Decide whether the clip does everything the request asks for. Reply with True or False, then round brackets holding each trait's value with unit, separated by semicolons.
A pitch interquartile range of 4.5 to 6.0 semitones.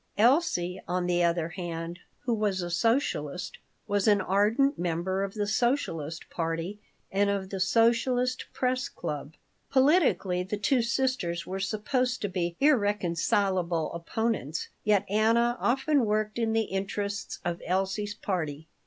True (4.8 semitones)